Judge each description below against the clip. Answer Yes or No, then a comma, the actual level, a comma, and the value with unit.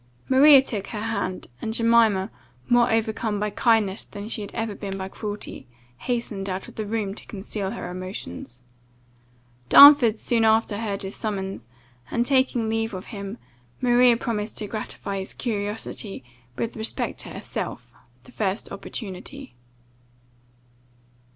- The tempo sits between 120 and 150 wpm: Yes, average, 140 wpm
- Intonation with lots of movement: No, average, 2.8 semitones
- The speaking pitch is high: Yes, high, 215 Hz